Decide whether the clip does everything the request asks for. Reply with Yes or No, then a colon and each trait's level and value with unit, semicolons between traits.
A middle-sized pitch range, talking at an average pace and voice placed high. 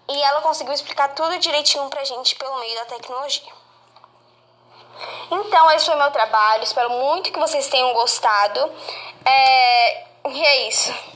Yes: average, 3.8 semitones; average, 145 wpm; very high, 285 Hz